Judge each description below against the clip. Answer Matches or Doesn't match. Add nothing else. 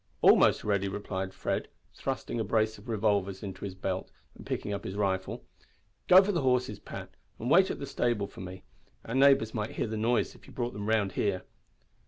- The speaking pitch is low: Matches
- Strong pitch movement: Doesn't match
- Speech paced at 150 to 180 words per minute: Doesn't match